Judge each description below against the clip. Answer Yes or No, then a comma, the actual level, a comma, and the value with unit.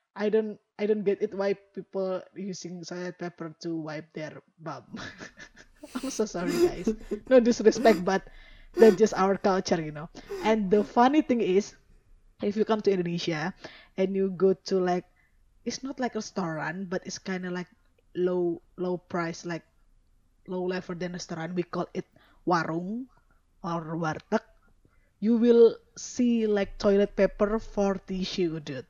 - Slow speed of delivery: No, average, 160 wpm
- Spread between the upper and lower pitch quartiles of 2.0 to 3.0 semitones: No, average, 4.0 semitones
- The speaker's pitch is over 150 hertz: Yes, high, 190 Hz